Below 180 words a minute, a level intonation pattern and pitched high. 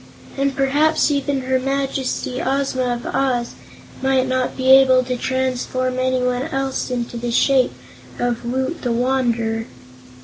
Yes: slow, 135 wpm; narrow, 1.4 semitones; very high, 260 Hz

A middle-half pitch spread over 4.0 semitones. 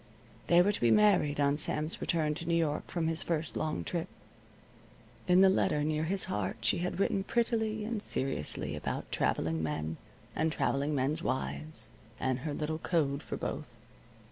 Yes: average, 4.4 semitones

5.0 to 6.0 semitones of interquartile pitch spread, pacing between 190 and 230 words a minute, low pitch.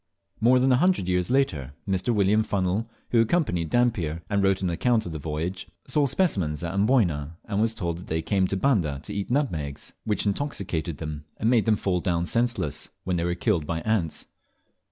Yes: wide, 5.5 semitones; average, 195 wpm; very low, 95 Hz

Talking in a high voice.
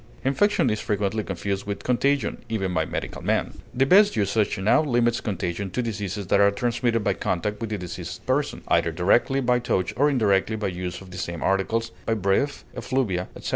No: low, 105 Hz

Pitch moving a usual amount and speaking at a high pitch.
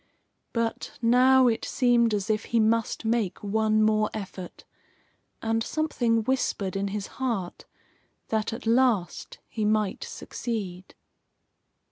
No: narrow, 2.0 semitones; high, 220 Hz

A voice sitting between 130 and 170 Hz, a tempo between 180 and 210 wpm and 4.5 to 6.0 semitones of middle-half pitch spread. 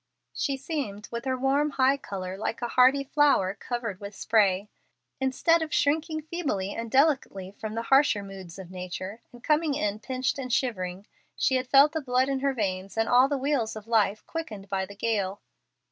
No: high, 240 Hz; average, 190 wpm; wide, 5.5 semitones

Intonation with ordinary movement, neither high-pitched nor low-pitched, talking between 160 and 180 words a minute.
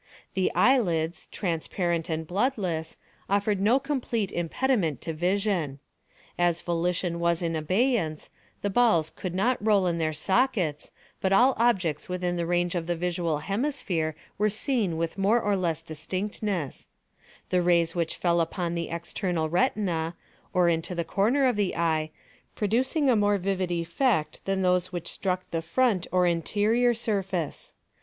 No: average, 3.8 semitones; medium, 180 Hz; average, 150 wpm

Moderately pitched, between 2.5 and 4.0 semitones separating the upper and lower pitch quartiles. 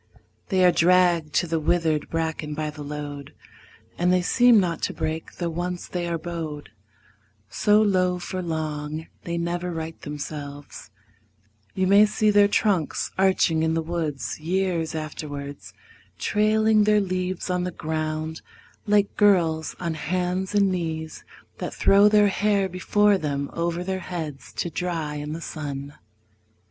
Yes: medium, 170 Hz; average, 3.1 semitones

